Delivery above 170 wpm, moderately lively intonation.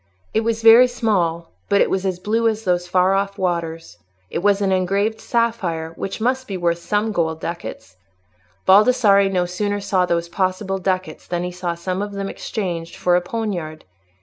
Yes: average, 180 wpm; average, 3.1 semitones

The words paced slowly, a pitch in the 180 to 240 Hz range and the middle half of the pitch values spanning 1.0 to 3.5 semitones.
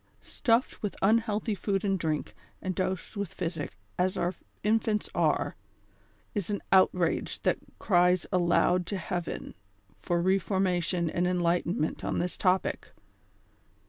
Yes: slow, 115 wpm; medium, 185 Hz; narrow, 2.5 semitones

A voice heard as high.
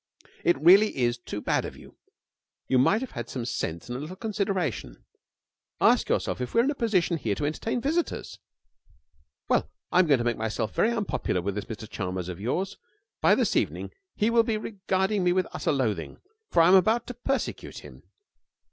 No: medium, 175 Hz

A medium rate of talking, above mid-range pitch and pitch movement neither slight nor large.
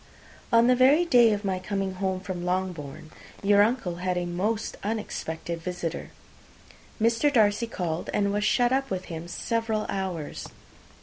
Yes: average, 150 wpm; high, 195 Hz; average, 4.2 semitones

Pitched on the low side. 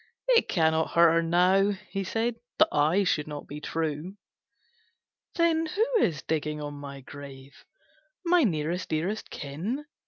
No: medium, 165 Hz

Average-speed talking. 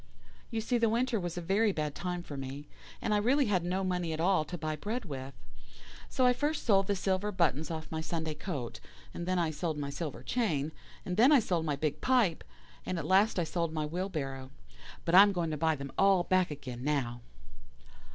No: fast, 220 wpm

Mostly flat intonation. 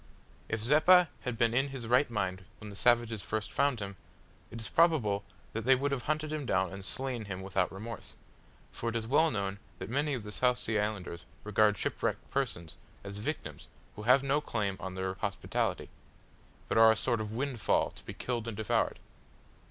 No: average, 4.6 semitones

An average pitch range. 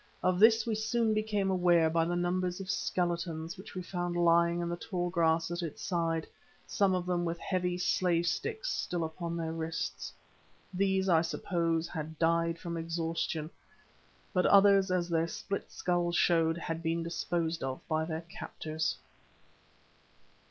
No: narrow, 1.8 semitones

